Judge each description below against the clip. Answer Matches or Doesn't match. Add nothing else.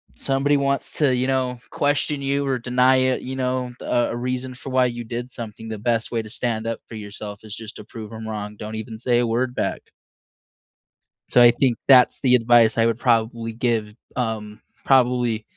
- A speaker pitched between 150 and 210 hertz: Doesn't match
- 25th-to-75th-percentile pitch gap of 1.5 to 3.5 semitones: Matches